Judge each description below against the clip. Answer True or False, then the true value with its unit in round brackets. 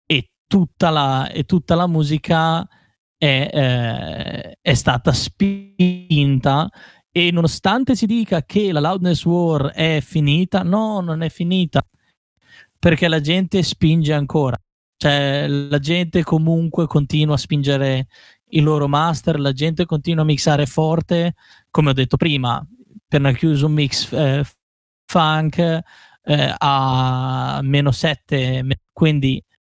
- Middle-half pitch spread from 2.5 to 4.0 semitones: True (3.4 semitones)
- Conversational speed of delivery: True (125 wpm)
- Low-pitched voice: False (155 Hz)